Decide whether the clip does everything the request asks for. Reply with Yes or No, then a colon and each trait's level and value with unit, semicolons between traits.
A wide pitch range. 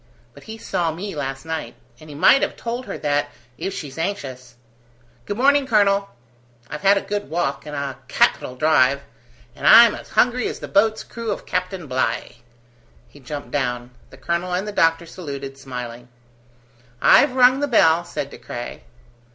Yes: wide, 6.7 semitones